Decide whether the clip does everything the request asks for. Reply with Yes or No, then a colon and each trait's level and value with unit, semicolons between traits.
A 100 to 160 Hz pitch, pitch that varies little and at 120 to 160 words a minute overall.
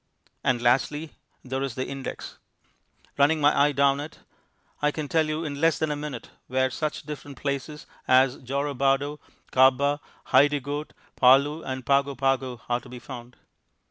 Yes: medium, 140 Hz; narrow, 2.0 semitones; average, 155 wpm